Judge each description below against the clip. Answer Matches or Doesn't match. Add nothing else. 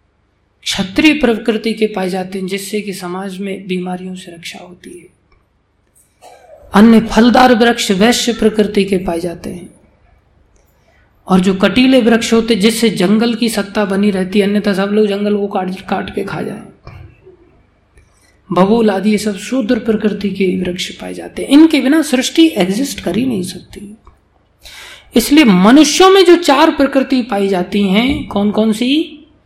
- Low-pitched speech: Doesn't match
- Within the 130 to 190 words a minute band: Matches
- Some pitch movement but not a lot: Matches